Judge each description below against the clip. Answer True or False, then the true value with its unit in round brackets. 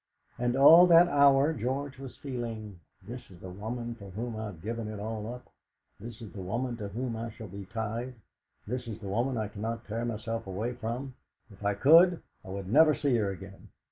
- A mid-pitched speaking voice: False (115 Hz)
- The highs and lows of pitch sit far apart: False (3.6 semitones)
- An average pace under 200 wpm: False (205 wpm)